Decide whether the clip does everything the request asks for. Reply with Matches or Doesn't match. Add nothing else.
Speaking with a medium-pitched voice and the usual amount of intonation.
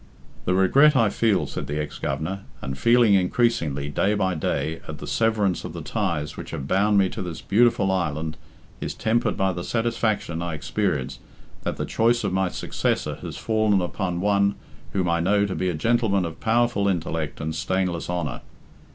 Doesn't match